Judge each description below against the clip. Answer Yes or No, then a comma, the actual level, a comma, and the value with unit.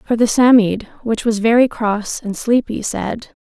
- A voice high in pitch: Yes, high, 225 Hz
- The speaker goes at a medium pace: Yes, average, 175 wpm